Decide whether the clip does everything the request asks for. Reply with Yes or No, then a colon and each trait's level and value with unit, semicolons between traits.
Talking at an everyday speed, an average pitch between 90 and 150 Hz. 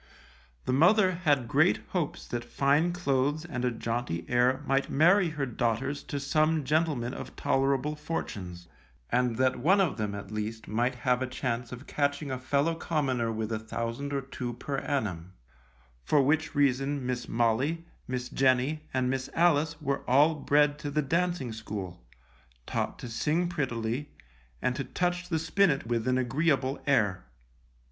Yes: average, 160 wpm; low, 135 Hz